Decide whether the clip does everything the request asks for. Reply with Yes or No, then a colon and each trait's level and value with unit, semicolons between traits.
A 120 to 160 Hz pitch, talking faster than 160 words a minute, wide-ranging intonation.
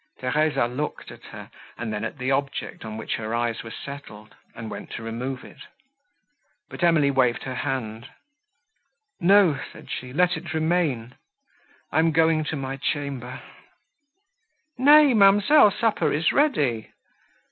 No: medium, 140 Hz; average, 140 wpm; wide, 6.8 semitones